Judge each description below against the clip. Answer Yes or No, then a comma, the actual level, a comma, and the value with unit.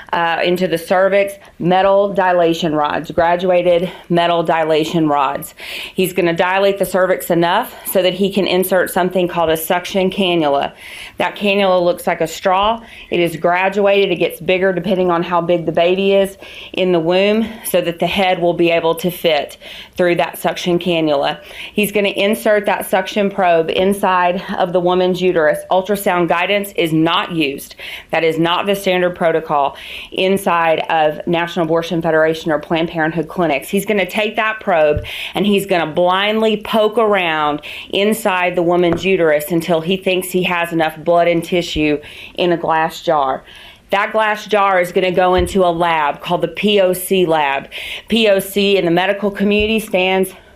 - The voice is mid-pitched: Yes, medium, 180 Hz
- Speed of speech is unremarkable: Yes, average, 170 wpm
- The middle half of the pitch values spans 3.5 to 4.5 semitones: No, narrow, 2.5 semitones